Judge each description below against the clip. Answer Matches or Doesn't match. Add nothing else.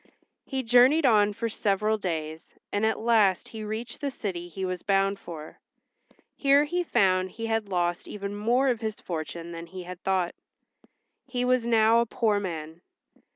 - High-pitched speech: Matches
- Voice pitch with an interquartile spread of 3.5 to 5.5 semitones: Matches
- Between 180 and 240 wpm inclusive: Doesn't match